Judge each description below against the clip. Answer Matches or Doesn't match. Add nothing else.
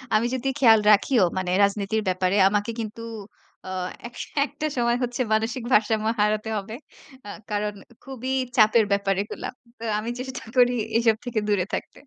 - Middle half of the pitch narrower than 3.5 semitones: Matches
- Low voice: Doesn't match